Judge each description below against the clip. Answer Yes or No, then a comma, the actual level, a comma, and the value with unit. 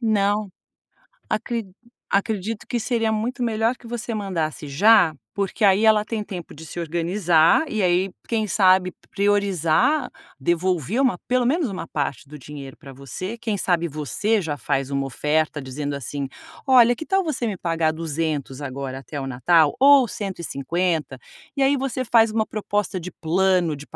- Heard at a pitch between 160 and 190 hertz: Yes, medium, 185 Hz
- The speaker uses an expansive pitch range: Yes, wide, 6.2 semitones